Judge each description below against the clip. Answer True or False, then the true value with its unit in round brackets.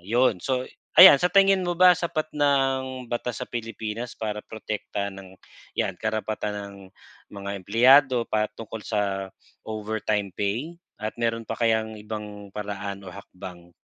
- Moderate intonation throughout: True (3.9 semitones)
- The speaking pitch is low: True (110 Hz)